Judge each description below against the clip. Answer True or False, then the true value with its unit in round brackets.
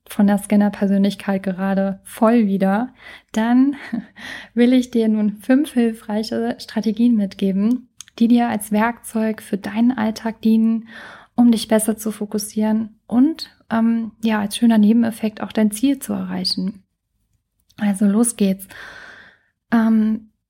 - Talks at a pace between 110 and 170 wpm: True (125 wpm)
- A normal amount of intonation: False (1.9 semitones)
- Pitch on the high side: True (220 Hz)